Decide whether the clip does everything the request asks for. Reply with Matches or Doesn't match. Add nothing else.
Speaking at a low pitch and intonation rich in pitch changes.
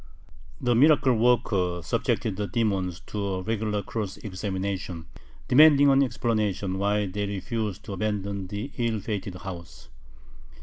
Doesn't match